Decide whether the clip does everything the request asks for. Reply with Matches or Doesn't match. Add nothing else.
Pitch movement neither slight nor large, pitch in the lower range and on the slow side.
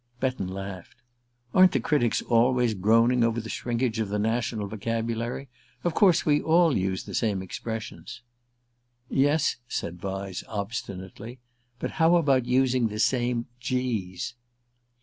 Matches